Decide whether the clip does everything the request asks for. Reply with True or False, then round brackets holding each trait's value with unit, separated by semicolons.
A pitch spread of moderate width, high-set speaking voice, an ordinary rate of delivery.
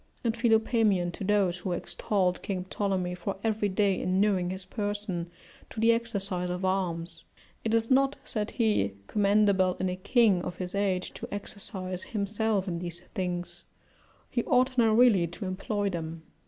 True (3.1 semitones; 195 Hz; 160 wpm)